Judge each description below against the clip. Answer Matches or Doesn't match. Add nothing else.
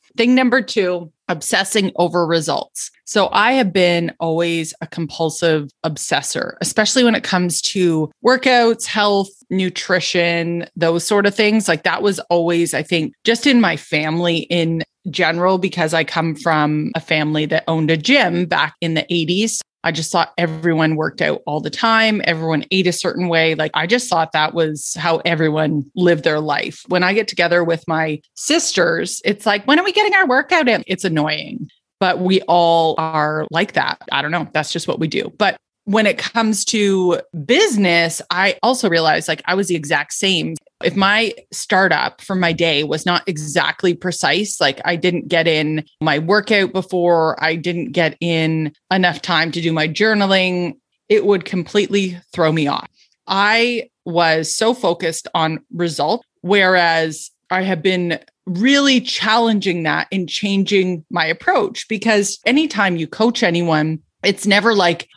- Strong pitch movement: Doesn't match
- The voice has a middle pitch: Matches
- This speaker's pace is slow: Doesn't match